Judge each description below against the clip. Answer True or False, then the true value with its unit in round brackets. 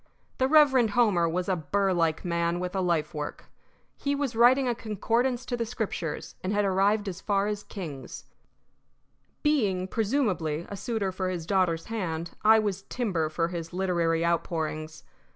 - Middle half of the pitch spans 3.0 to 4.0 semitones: False (4.8 semitones)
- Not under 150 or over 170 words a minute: True (165 wpm)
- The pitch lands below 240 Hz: True (190 Hz)